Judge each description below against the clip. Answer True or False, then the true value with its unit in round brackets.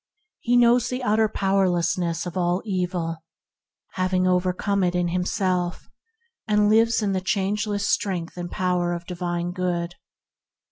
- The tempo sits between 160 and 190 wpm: False (135 wpm)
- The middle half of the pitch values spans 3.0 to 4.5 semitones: False (2.5 semitones)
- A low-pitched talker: False (185 Hz)